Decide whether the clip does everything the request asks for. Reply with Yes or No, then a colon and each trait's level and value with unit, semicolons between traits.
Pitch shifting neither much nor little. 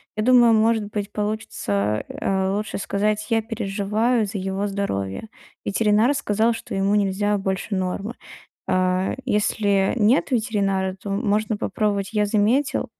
No: narrow, 2.0 semitones